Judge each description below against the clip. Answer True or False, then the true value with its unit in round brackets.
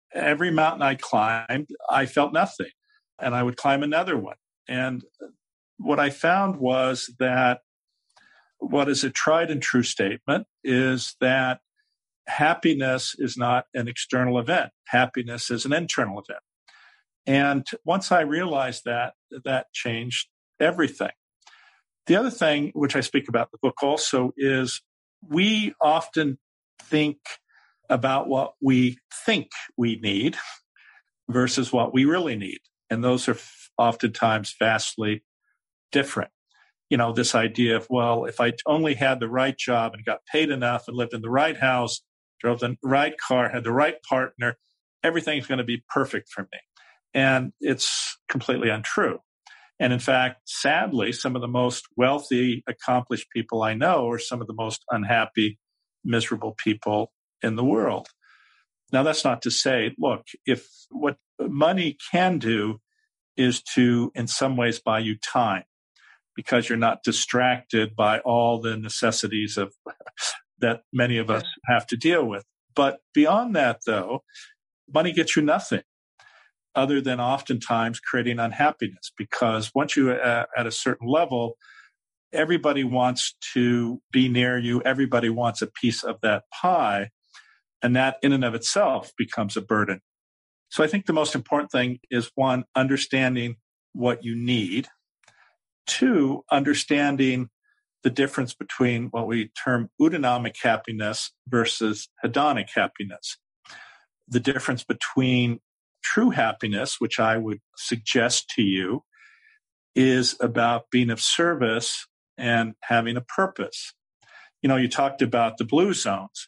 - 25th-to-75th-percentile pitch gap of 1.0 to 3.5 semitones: True (2.9 semitones)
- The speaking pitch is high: False (125 Hz)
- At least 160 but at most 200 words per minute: False (140 wpm)